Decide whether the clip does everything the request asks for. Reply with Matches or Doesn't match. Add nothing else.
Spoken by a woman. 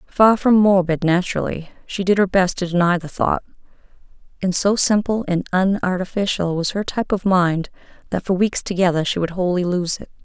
Matches